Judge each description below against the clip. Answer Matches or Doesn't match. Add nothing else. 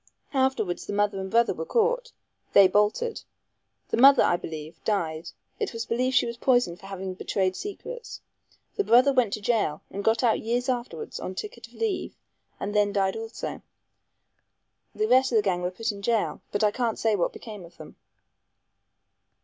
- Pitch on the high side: Matches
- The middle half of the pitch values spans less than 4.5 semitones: Doesn't match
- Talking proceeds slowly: Doesn't match